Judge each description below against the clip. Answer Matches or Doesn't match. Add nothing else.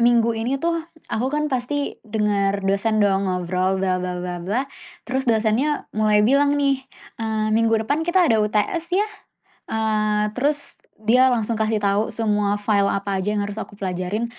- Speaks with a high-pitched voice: Matches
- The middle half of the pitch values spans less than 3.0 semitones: Doesn't match